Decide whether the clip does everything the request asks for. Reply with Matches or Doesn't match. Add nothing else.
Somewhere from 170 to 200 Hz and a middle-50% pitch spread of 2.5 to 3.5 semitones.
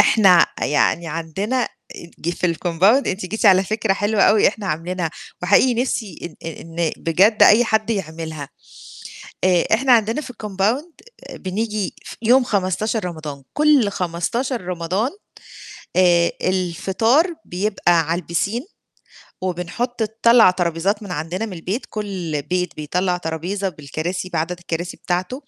Doesn't match